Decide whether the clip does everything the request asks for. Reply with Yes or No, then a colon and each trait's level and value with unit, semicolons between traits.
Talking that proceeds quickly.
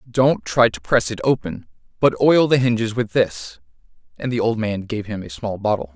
Yes: fast, 210 wpm